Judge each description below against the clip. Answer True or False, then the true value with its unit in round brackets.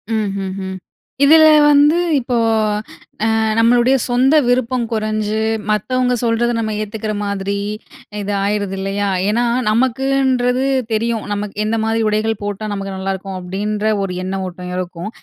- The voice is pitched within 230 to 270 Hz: False (215 Hz)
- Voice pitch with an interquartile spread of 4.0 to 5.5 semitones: False (3.6 semitones)